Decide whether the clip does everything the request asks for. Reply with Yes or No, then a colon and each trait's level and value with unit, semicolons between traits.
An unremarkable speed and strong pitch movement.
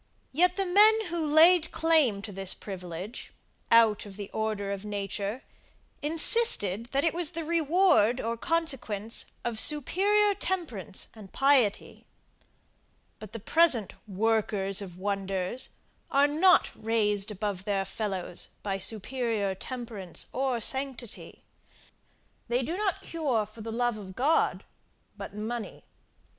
No: slow, 125 wpm; wide, 7.3 semitones